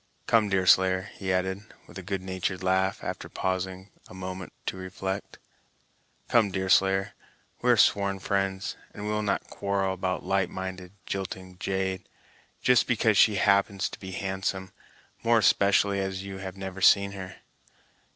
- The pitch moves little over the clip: Yes, narrow, 1.0 semitones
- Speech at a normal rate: Yes, average, 150 wpm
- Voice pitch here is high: No, very low, 95 Hz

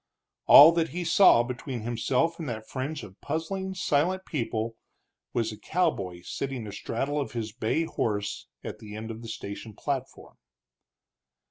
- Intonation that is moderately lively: No, wide, 6.4 semitones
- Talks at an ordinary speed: Yes, average, 150 wpm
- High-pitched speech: No, low, 125 Hz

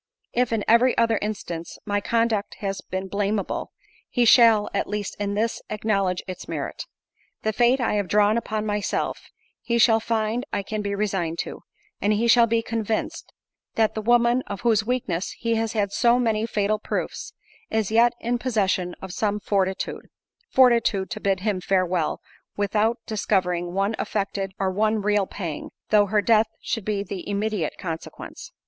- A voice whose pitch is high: Yes, high, 210 Hz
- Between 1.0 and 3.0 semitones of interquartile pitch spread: Yes, narrow, 2.5 semitones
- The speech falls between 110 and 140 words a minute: No, average, 165 wpm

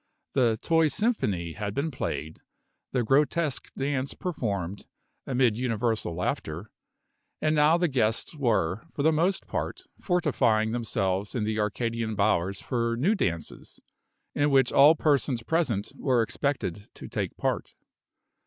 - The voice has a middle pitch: No, low, 120 Hz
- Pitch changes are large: Yes, wide, 5.7 semitones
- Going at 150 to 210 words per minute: No, slow, 135 wpm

